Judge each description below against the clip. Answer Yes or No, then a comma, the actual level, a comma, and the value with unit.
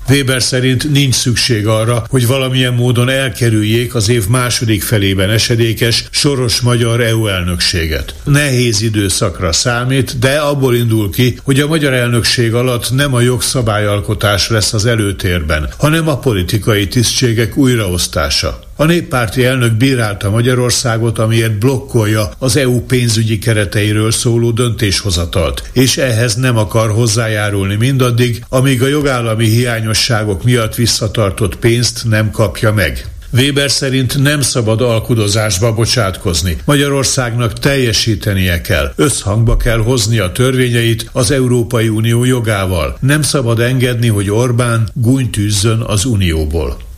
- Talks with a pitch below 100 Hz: No, low, 115 Hz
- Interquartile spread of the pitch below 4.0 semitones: Yes, average, 2.9 semitones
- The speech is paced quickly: No, average, 125 wpm